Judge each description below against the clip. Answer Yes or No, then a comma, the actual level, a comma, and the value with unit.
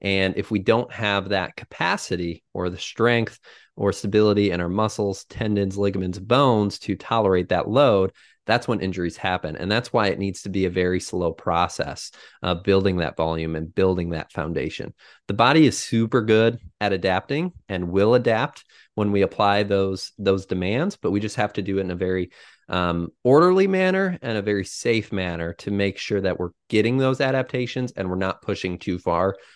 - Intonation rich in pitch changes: No, average, 3.2 semitones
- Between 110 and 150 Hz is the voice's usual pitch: No, low, 100 Hz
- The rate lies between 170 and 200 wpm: Yes, average, 190 wpm